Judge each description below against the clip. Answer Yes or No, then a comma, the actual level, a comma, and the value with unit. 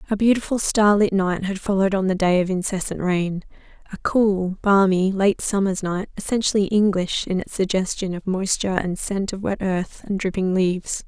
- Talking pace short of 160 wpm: No, average, 180 wpm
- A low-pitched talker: No, high, 195 Hz